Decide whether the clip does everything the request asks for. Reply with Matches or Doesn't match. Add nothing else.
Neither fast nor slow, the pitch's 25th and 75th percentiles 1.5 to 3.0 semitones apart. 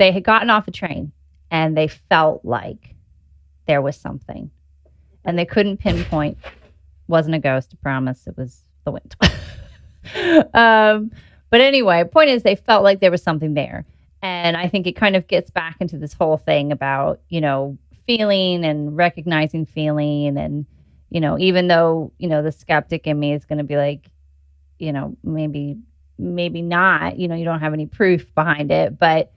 Doesn't match